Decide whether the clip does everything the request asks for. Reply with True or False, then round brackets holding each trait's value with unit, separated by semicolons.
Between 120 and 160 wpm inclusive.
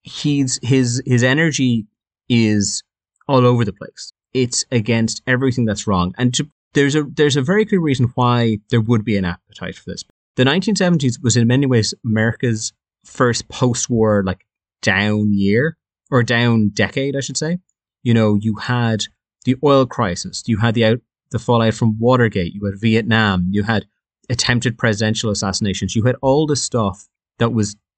False (170 wpm)